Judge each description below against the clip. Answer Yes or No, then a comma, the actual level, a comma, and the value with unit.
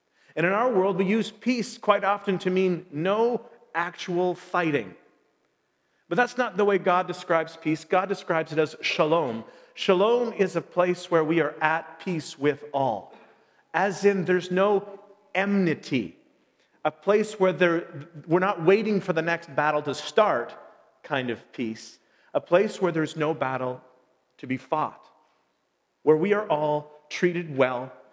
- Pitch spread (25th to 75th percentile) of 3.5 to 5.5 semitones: Yes, average, 4.4 semitones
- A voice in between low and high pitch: Yes, medium, 180 Hz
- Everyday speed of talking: Yes, average, 160 wpm